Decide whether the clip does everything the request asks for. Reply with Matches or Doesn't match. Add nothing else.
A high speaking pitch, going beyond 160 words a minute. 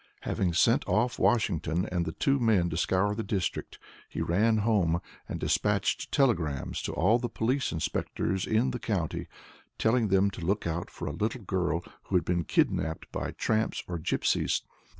Doesn't match